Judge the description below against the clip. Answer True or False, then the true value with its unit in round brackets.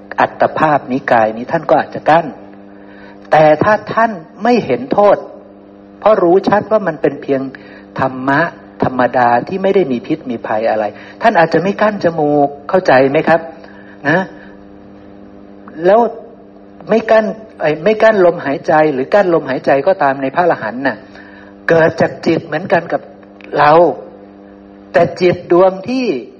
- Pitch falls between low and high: True (155 Hz)